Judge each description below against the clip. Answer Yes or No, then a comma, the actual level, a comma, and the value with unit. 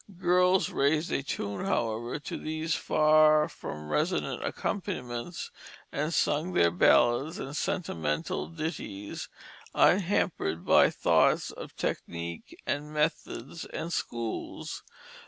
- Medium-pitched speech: Yes, medium, 150 Hz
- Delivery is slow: Yes, slow, 105 wpm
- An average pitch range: No, wide, 6.4 semitones